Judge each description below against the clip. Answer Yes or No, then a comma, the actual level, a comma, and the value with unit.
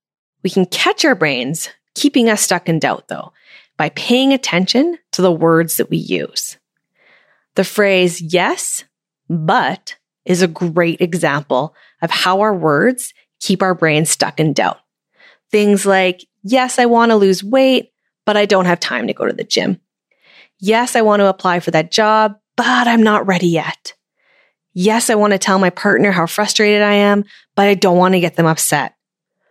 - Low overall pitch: No, high, 195 Hz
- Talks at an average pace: Yes, average, 180 wpm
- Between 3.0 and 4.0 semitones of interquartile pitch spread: Yes, average, 3.7 semitones